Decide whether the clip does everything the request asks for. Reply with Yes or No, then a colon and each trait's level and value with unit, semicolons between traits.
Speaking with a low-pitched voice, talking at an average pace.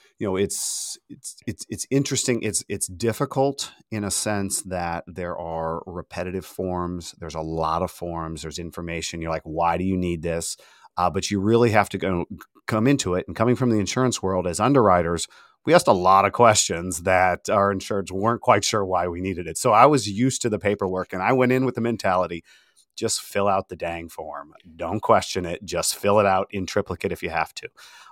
No: very low, 95 Hz; fast, 210 wpm